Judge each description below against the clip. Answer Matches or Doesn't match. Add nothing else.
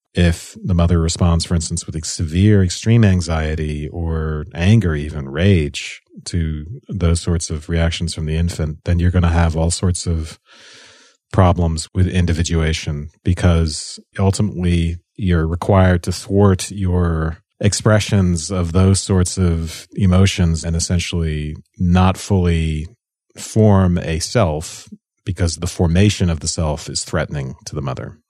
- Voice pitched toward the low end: Matches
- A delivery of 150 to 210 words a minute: Doesn't match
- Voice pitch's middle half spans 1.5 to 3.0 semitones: Matches